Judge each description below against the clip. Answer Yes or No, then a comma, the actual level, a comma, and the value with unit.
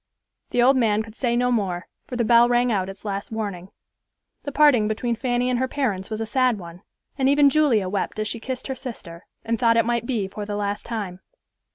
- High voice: Yes, high, 230 Hz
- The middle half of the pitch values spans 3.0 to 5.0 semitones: Yes, average, 3.4 semitones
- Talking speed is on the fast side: Yes, fast, 225 wpm